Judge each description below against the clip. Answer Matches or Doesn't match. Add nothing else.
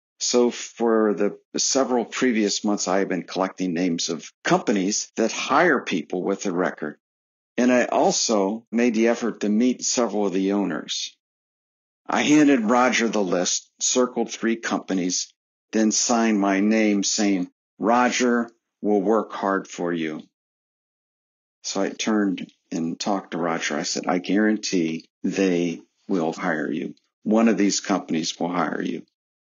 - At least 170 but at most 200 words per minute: Doesn't match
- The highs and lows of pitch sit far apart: Doesn't match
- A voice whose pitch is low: Matches